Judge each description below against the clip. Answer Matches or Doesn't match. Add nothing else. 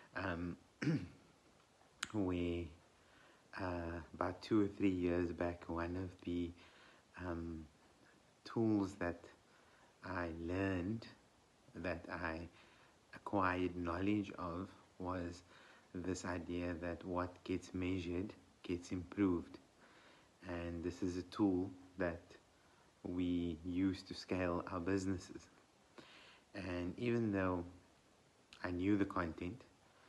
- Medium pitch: Doesn't match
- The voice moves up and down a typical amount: Doesn't match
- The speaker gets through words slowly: Matches